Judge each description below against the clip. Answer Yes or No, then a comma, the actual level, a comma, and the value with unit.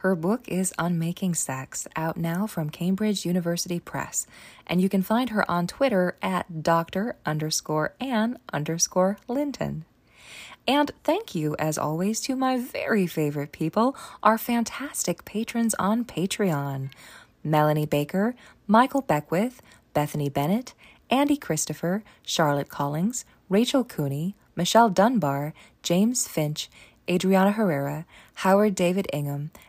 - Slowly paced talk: Yes, slow, 125 wpm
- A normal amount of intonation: No, wide, 6.0 semitones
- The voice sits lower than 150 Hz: No, medium, 185 Hz